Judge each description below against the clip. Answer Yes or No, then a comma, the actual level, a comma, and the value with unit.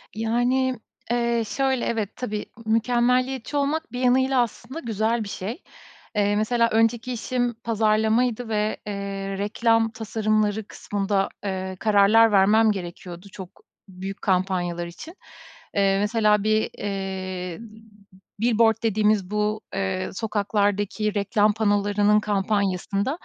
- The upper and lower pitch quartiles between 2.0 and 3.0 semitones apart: Yes, narrow, 2.6 semitones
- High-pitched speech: Yes, high, 215 Hz